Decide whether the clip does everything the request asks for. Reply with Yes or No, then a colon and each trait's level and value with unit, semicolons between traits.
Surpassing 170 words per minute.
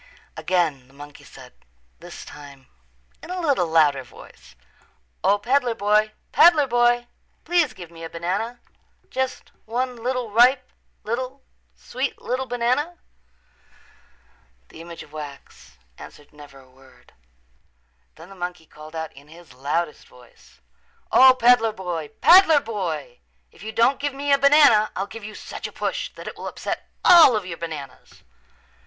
No: average, 150 wpm